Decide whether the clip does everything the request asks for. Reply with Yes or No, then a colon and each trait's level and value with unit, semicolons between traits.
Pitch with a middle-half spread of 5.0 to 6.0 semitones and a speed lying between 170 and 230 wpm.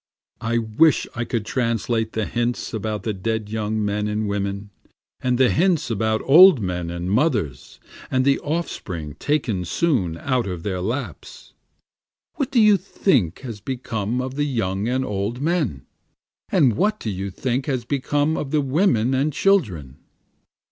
No: wide, 5.5 semitones; average, 160 wpm